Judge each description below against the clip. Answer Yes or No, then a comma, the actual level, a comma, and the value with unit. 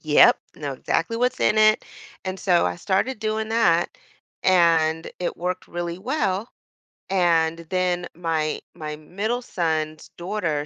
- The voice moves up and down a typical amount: Yes, average, 4.6 semitones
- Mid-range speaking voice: Yes, medium, 175 Hz